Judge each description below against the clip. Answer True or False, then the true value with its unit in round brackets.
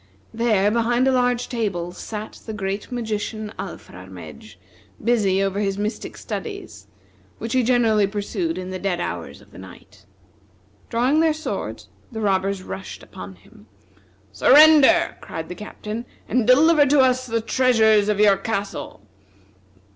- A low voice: False (215 Hz)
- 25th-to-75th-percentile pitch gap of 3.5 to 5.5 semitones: True (4.1 semitones)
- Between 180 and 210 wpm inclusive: False (140 wpm)